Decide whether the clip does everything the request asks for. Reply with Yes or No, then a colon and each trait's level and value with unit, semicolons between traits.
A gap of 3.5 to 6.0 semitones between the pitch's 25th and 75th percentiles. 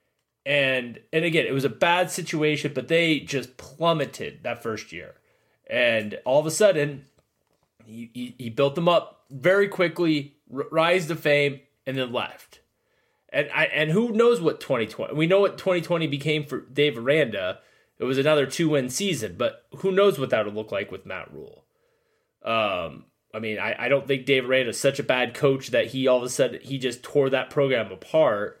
Yes: average, 4.2 semitones